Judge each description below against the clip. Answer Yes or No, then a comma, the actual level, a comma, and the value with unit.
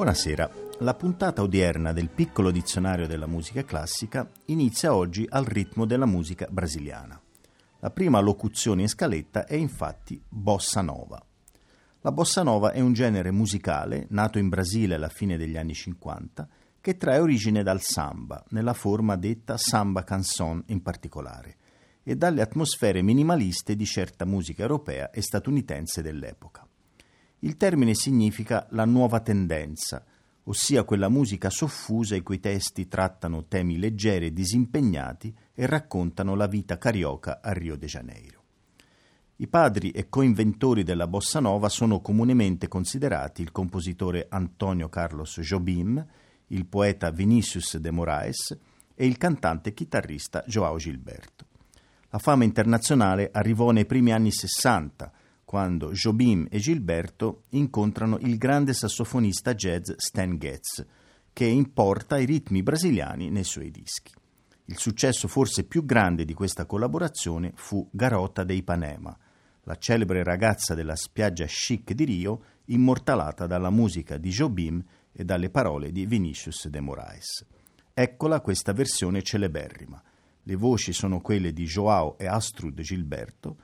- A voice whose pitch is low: Yes, low, 100 Hz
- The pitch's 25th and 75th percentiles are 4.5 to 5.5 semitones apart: Yes, average, 5.0 semitones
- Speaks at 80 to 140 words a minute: Yes, average, 135 wpm